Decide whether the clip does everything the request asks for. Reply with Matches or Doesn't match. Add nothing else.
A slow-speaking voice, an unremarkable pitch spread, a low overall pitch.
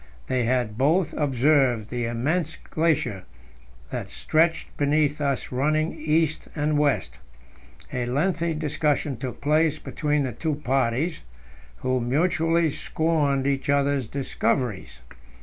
Doesn't match